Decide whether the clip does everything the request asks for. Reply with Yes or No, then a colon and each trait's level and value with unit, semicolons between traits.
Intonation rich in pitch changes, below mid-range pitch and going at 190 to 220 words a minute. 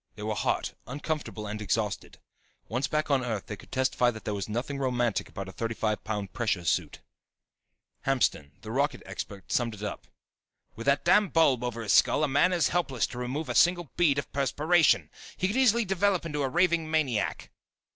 Yes: wide, 6.3 semitones; low, 130 Hz; average, 195 wpm